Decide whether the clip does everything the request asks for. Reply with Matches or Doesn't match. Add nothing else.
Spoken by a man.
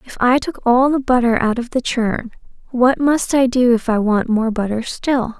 Doesn't match